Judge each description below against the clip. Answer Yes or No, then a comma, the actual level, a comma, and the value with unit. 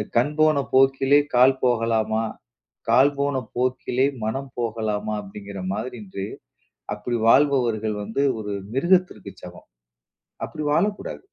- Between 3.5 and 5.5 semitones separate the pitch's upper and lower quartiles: Yes, average, 3.9 semitones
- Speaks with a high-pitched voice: No, low, 125 Hz